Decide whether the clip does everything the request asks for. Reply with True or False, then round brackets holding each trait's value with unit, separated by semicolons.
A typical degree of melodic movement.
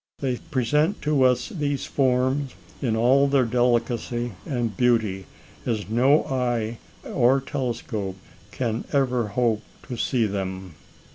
True (3.0 semitones)